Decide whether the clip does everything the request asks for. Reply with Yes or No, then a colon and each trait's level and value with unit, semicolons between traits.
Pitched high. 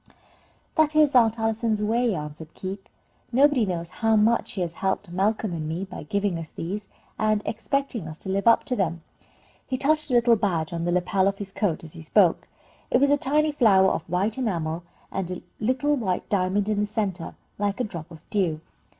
Yes: high, 200 Hz